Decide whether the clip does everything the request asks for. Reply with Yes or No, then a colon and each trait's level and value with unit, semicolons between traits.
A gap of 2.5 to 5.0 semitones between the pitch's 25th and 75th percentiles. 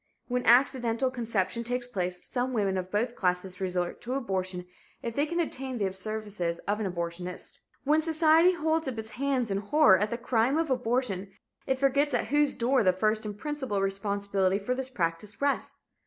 No: wide, 5.4 semitones